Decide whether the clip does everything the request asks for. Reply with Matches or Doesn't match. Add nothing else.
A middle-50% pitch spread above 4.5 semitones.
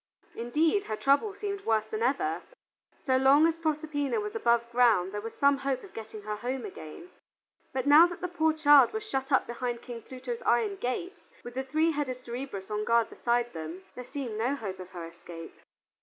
Matches